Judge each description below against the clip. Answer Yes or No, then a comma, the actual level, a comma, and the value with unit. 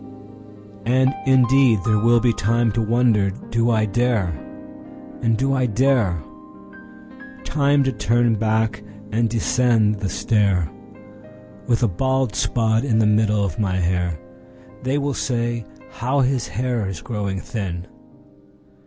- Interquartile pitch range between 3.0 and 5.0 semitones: Yes, average, 3.5 semitones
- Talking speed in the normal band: No, slow, 120 wpm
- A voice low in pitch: Yes, low, 115 Hz